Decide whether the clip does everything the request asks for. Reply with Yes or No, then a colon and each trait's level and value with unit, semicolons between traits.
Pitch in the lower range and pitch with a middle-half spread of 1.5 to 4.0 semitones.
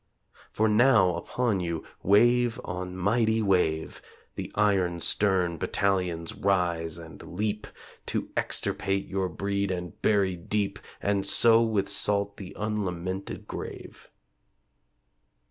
Yes: low, 100 Hz; average, 2.8 semitones